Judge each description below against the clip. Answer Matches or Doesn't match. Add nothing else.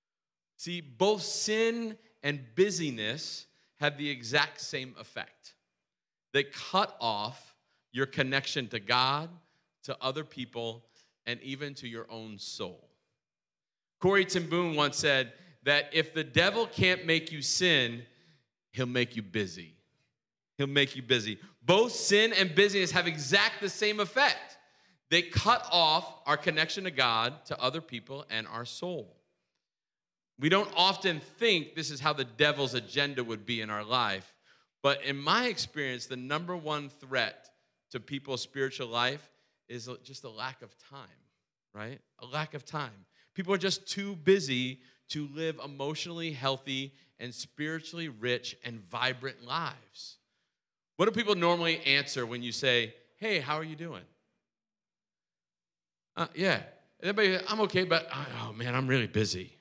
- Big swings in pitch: Matches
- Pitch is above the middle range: Doesn't match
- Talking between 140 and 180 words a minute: Matches